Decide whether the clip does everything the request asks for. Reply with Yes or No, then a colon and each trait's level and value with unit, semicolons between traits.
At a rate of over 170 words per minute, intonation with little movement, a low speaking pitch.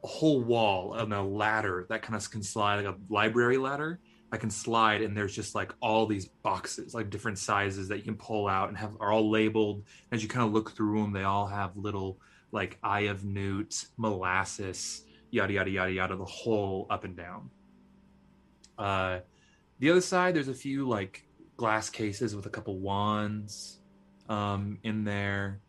Yes: average, 185 wpm; narrow, 2.0 semitones; low, 105 Hz